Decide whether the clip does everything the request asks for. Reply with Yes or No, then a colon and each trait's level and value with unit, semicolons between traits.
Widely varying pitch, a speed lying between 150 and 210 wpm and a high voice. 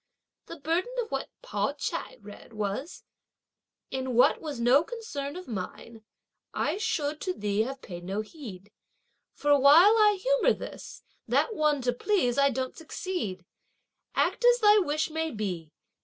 Yes: wide, 8.3 semitones; average, 155 wpm; very high, 285 Hz